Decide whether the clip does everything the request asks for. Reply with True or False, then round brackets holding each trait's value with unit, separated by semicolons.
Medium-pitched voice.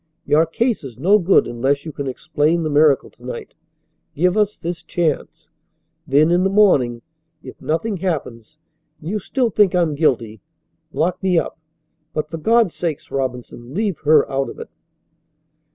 True (160 Hz)